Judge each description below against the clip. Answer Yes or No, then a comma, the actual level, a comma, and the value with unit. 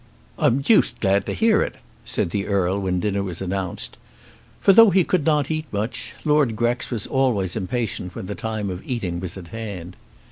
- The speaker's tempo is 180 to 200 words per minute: Yes, average, 190 wpm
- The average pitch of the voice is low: Yes, low, 105 Hz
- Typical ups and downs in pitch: No, wide, 5.9 semitones